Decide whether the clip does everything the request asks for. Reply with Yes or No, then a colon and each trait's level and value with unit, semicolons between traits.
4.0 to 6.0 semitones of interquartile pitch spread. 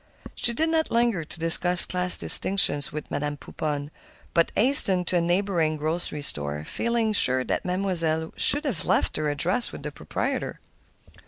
Yes: average, 4.9 semitones